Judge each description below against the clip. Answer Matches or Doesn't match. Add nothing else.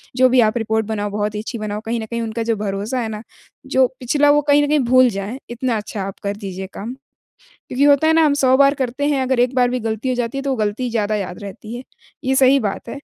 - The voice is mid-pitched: Doesn't match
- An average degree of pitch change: Matches